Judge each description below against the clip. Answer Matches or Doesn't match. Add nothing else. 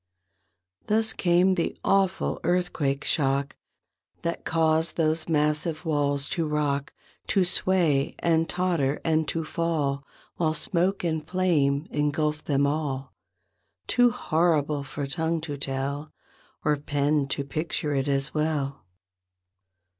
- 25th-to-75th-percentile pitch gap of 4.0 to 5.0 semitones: Doesn't match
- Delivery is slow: Matches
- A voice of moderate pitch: Matches